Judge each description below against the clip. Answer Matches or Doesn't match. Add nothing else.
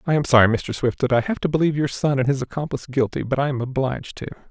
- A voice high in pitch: Doesn't match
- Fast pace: Matches